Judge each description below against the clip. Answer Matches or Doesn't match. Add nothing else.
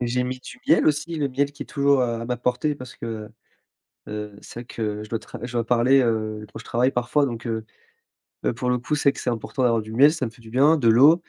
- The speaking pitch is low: Matches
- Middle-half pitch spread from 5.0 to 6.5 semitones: Doesn't match